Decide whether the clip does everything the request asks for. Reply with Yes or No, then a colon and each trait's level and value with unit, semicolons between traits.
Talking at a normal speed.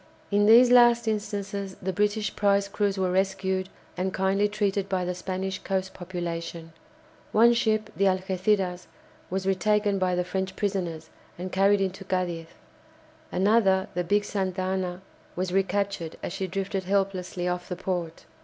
Yes: average, 150 wpm